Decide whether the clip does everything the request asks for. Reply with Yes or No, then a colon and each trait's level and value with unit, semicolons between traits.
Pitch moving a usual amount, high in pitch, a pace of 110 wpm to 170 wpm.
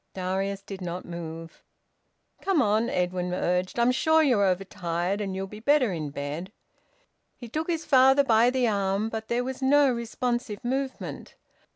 No: wide, 5.7 semitones; high, 215 Hz; average, 160 wpm